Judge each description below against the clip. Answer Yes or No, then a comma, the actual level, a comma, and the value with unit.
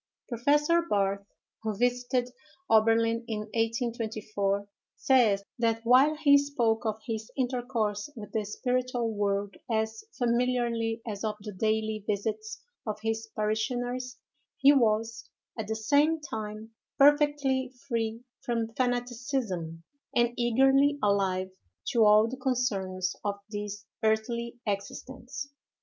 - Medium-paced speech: No, slow, 115 wpm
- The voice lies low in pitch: No, high, 225 Hz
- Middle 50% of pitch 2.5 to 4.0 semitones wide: Yes, average, 2.9 semitones